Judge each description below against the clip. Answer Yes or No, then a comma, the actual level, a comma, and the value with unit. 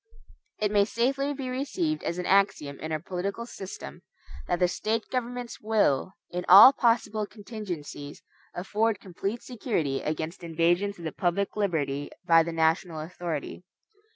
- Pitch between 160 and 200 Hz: Yes, high, 190 Hz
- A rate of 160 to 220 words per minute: No, average, 145 wpm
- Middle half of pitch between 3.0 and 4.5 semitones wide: No, average, 5.2 semitones